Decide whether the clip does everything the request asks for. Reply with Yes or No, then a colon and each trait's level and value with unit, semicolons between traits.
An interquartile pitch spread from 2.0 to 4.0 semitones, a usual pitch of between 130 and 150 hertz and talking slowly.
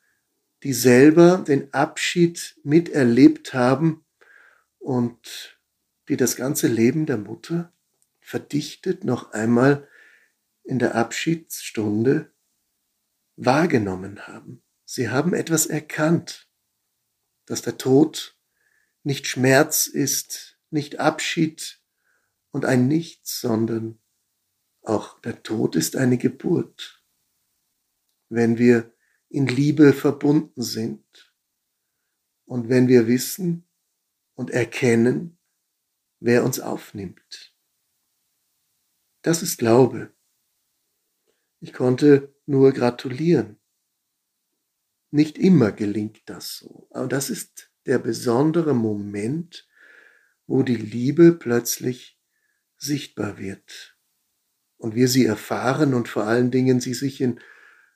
No: average, 5.1 semitones; low, 135 Hz; slow, 95 wpm